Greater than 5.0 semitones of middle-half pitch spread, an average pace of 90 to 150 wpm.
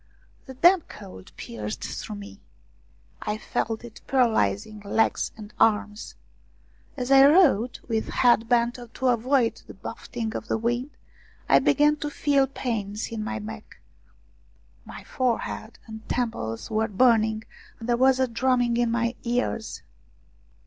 No: narrow, 2.6 semitones; average, 140 wpm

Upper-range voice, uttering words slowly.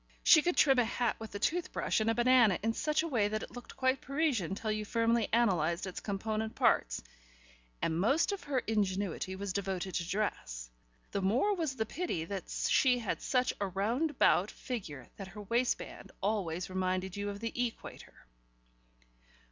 No: high, 215 Hz; average, 180 wpm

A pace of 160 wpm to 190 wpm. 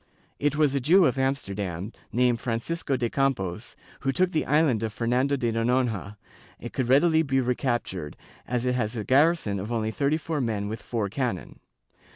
Yes: average, 185 wpm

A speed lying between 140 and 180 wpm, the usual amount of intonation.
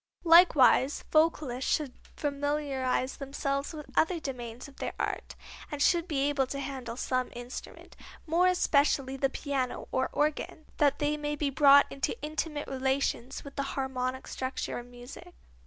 No: average, 150 wpm; narrow, 2.3 semitones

